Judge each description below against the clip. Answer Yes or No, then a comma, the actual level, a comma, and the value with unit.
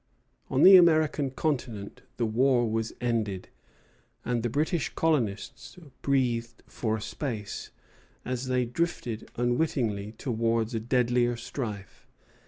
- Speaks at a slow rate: Yes, slow, 115 wpm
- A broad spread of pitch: No, average, 3.2 semitones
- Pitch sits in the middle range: No, low, 120 Hz